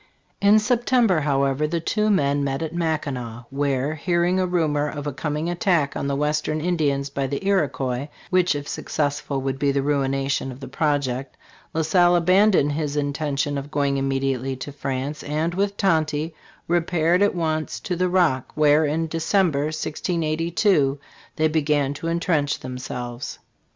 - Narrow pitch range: No, average, 3.5 semitones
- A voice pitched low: No, medium, 150 Hz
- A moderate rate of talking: Yes, average, 160 wpm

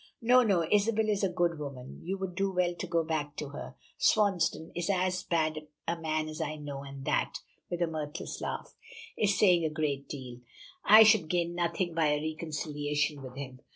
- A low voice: No, medium, 165 Hz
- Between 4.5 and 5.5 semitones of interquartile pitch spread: No, average, 3.6 semitones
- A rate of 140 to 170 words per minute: No, average, 195 wpm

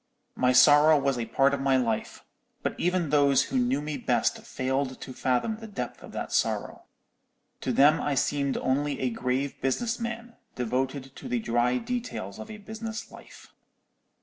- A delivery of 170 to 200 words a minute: Yes, average, 175 wpm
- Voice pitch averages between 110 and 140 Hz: Yes, low, 135 Hz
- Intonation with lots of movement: No, average, 3.5 semitones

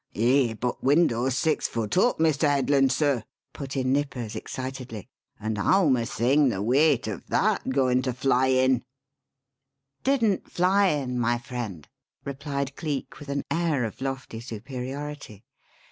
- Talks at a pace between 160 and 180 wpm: No, average, 145 wpm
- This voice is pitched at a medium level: No, low, 130 Hz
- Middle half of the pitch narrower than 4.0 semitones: Yes, average, 3.1 semitones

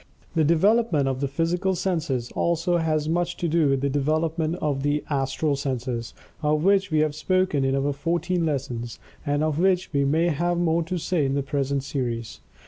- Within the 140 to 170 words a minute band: No, average, 190 wpm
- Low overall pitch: No, medium, 155 Hz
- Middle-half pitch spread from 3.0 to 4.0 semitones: Yes, average, 3.6 semitones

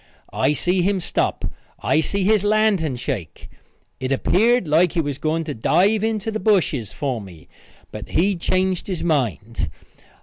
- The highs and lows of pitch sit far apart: Yes, wide, 6.5 semitones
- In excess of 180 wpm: No, average, 160 wpm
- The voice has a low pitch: No, medium, 170 Hz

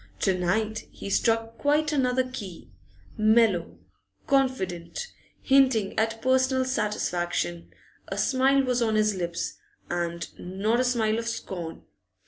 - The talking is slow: Yes, slow, 120 wpm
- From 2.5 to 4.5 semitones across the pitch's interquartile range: No, wide, 5.6 semitones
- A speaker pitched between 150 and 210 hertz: No, high, 220 Hz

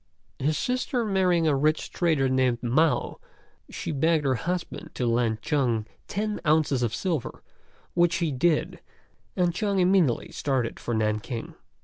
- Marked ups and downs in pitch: Yes, wide, 6.0 semitones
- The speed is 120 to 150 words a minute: Yes, average, 140 wpm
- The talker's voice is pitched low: No, medium, 150 Hz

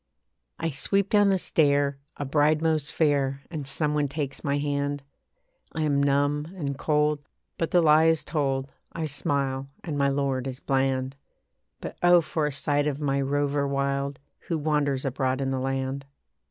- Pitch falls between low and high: Yes, medium, 145 Hz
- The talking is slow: No, average, 170 wpm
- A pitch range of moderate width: No, narrow, 1.8 semitones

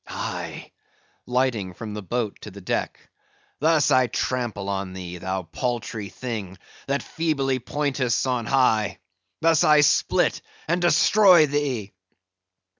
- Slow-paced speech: Yes, slow, 125 wpm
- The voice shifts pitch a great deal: Yes, wide, 6.2 semitones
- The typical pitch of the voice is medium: No, low, 125 Hz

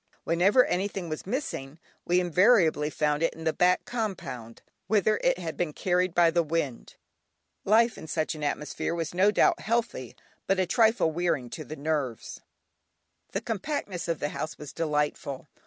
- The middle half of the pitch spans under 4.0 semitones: No, average, 4.5 semitones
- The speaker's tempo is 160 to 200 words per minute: Yes, average, 165 wpm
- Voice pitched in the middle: Yes, medium, 170 Hz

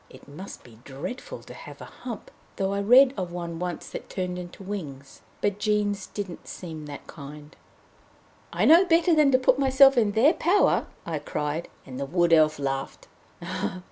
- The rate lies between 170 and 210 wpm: Yes, average, 175 wpm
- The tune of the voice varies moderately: No, wide, 8.3 semitones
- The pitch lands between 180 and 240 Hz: Yes, medium, 185 Hz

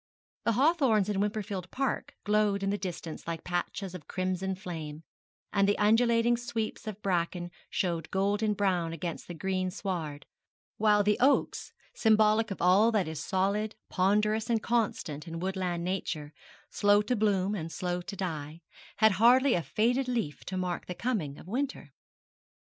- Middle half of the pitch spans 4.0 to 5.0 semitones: No, average, 3.5 semitones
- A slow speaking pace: No, average, 160 wpm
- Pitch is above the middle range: Yes, high, 195 Hz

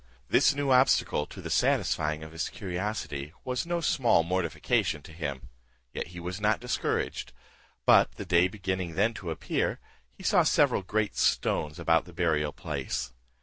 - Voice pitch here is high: No, very low, 90 Hz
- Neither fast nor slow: Yes, average, 160 wpm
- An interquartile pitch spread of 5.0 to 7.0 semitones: Yes, average, 5.3 semitones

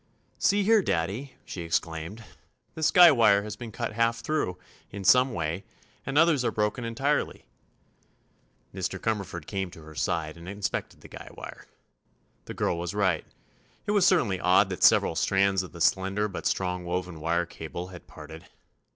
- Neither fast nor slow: Yes, average, 170 wpm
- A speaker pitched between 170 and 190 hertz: No, very low, 95 Hz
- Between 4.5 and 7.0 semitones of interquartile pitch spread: Yes, average, 5.0 semitones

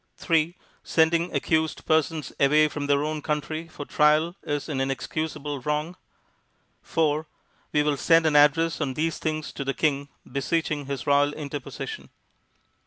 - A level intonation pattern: Yes, narrow, 1.8 semitones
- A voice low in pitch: No, medium, 150 Hz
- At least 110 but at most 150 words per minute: Yes, average, 145 wpm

